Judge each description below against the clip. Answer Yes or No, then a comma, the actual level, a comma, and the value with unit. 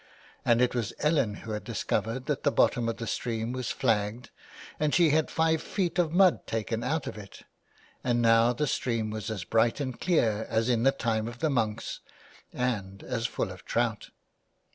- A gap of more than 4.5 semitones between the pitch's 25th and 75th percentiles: No, average, 3.8 semitones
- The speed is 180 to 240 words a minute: Yes, average, 190 wpm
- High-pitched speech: No, low, 120 Hz